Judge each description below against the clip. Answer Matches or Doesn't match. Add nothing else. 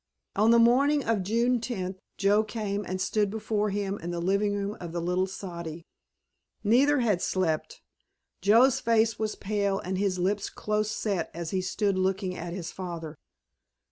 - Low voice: Doesn't match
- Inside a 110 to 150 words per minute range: Doesn't match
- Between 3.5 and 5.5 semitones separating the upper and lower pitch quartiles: Doesn't match